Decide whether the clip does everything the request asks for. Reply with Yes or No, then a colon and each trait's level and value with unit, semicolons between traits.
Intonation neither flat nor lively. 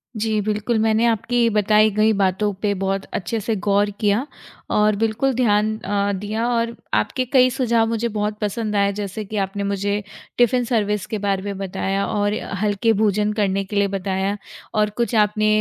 No: narrow, 1.9 semitones